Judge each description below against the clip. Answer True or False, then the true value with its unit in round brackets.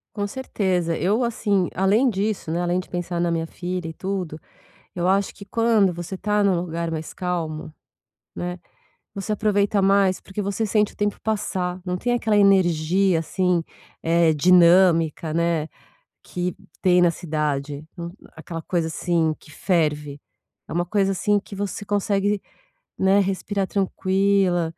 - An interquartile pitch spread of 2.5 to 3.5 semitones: True (3.1 semitones)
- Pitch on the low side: False (185 Hz)